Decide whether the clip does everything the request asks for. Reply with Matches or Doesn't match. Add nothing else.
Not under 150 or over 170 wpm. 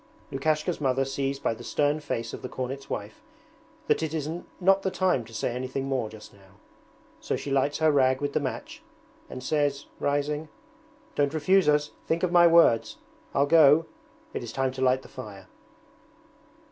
Doesn't match